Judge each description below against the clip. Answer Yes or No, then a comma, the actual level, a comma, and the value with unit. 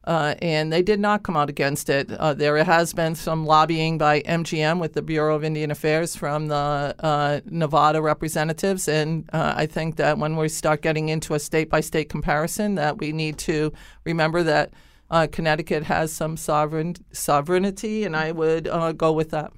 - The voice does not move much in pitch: Yes, narrow, 1.4 semitones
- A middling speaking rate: Yes, average, 185 wpm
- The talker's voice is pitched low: No, medium, 155 Hz